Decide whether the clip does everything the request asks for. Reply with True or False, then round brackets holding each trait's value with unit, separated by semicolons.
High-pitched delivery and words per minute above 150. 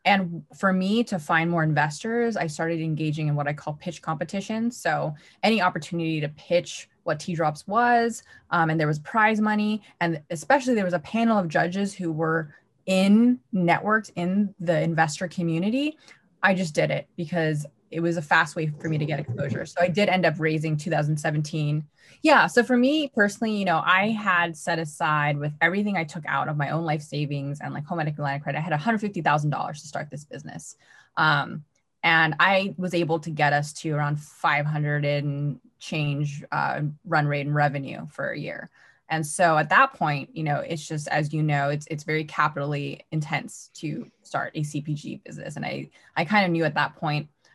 False (160 Hz; 195 wpm)